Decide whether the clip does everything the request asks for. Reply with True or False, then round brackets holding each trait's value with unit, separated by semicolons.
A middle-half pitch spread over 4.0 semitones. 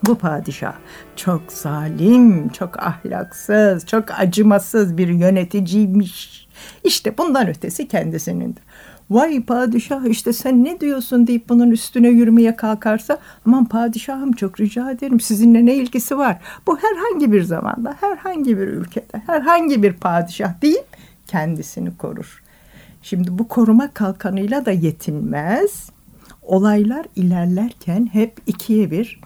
True (4.6 semitones)